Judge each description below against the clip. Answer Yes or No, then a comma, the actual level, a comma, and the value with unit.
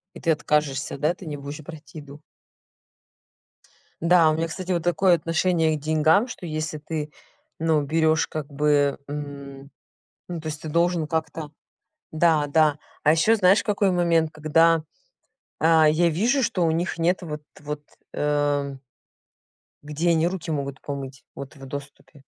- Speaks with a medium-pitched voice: Yes, medium, 155 Hz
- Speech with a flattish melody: Yes, narrow, 2.3 semitones